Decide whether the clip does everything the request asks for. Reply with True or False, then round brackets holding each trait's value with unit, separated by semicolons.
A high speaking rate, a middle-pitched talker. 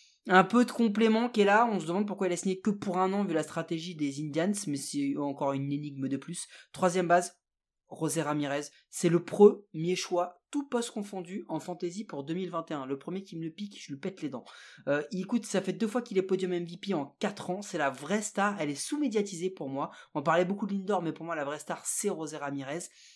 True (240 wpm; 180 Hz)